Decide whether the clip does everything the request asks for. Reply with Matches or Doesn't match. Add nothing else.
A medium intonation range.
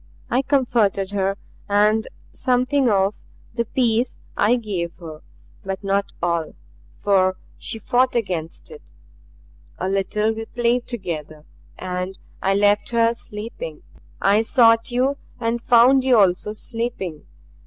Matches